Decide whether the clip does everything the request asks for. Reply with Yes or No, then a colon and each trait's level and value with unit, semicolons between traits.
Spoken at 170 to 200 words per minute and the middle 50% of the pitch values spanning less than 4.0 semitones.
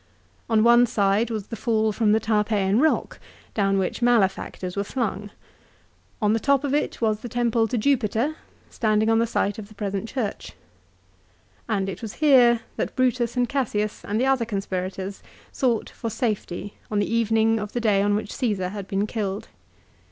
Yes: average, 180 wpm; average, 2.7 semitones